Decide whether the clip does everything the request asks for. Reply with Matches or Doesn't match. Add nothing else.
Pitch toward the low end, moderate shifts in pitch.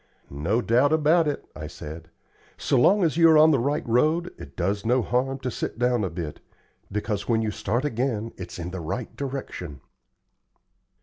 Doesn't match